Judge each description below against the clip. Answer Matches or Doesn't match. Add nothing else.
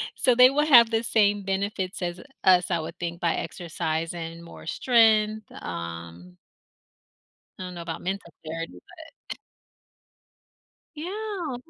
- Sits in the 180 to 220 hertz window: Matches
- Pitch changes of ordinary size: Doesn't match